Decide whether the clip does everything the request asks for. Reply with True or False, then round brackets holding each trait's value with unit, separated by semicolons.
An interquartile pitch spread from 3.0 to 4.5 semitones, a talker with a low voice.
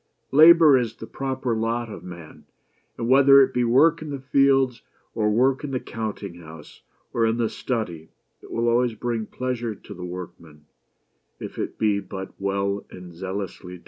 False (5.1 semitones; 115 Hz)